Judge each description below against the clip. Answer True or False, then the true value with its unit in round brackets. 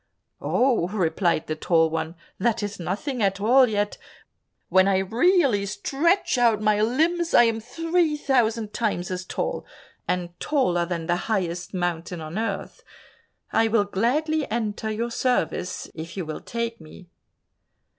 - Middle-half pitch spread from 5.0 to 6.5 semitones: True (5.3 semitones)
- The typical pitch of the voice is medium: False (210 Hz)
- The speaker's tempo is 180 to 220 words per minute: False (145 wpm)